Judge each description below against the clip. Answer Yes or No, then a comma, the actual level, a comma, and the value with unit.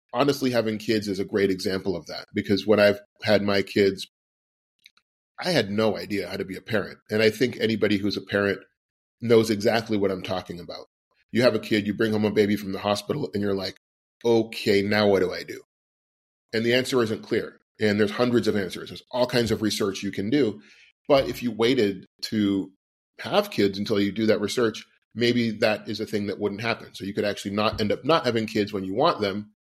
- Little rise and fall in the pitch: Yes, narrow, 2.2 semitones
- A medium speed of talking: No, fast, 220 wpm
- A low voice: Yes, low, 105 Hz